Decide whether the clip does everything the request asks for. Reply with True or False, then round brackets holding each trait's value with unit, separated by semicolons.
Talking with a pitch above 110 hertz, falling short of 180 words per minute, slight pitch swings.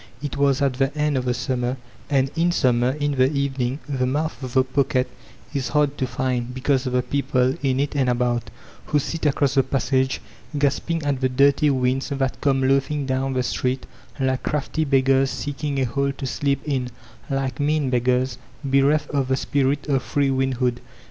False (135 Hz; 190 wpm; 1.7 semitones)